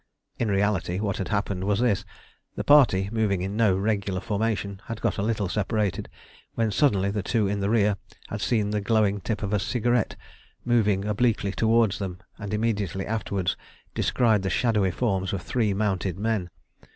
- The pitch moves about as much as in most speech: No, narrow, 2.3 semitones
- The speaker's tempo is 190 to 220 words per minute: No, average, 175 wpm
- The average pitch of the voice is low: Yes, low, 105 Hz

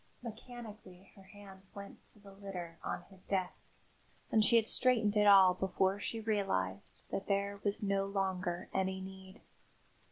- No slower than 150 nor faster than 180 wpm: Yes, average, 155 wpm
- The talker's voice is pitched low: No, high, 195 Hz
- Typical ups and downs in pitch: No, narrow, 1.6 semitones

